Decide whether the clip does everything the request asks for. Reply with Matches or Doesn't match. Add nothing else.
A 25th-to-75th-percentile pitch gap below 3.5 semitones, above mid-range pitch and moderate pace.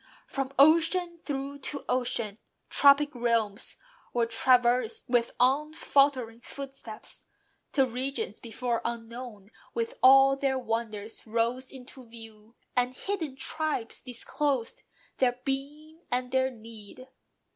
Doesn't match